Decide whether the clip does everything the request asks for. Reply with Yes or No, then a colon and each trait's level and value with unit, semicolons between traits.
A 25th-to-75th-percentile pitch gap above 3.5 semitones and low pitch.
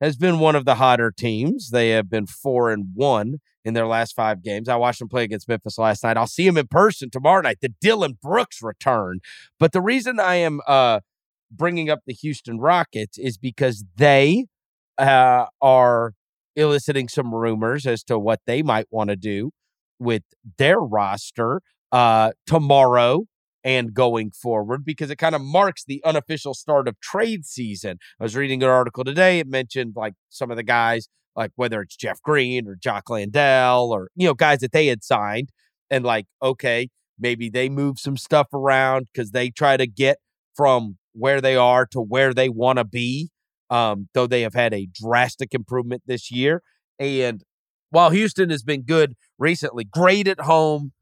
Yes: average, 4.1 semitones; low, 130 Hz